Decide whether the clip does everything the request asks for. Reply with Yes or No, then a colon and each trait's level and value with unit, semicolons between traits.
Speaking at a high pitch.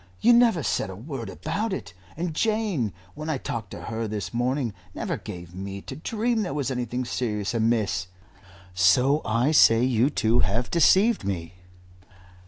No: low, 120 Hz